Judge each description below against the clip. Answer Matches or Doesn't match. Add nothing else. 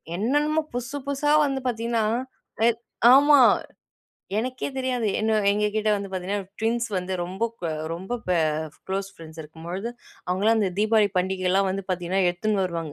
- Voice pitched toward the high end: Matches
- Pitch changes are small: Doesn't match